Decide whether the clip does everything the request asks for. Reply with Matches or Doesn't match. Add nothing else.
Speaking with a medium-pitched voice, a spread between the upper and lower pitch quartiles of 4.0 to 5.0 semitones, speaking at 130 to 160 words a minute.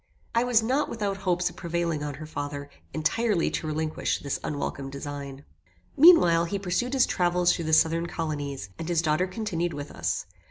Doesn't match